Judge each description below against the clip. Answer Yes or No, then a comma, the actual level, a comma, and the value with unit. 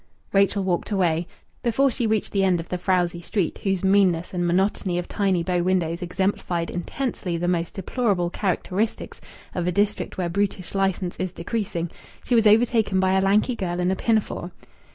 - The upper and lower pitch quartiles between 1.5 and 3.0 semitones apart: Yes, narrow, 2.5 semitones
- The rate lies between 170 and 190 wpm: Yes, average, 175 wpm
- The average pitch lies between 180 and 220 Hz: Yes, medium, 185 Hz